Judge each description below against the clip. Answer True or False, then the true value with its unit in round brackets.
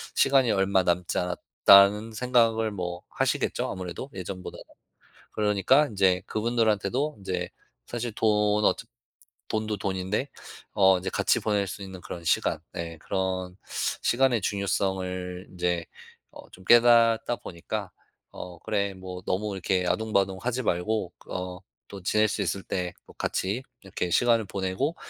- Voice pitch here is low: True (100 Hz)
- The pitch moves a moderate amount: True (3.2 semitones)